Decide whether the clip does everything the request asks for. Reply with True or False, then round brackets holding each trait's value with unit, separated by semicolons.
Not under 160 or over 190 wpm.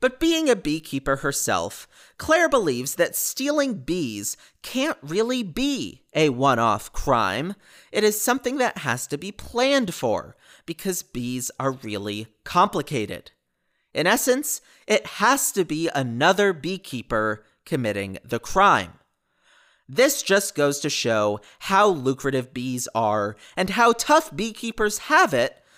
False (135 wpm)